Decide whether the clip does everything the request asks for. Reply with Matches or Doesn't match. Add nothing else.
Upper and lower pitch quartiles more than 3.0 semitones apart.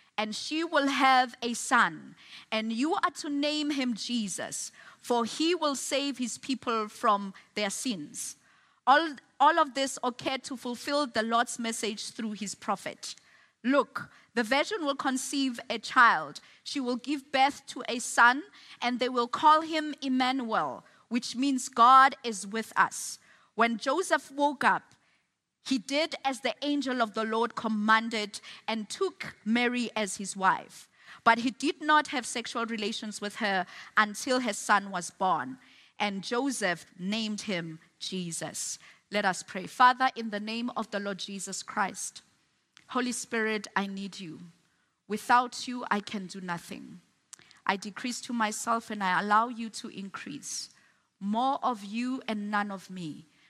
Matches